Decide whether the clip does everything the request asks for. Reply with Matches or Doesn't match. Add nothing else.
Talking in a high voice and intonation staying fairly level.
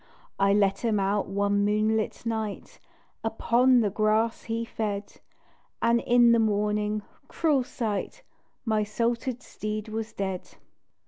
Matches